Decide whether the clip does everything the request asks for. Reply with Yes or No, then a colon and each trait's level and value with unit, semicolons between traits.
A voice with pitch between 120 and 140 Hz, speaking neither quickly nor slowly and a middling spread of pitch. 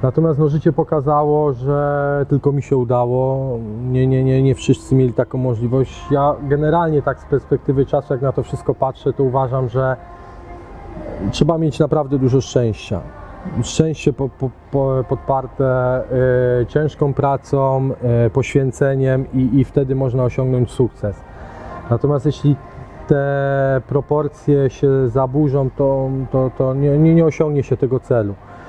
No: low, 135 Hz; average, 140 wpm; narrow, 1.9 semitones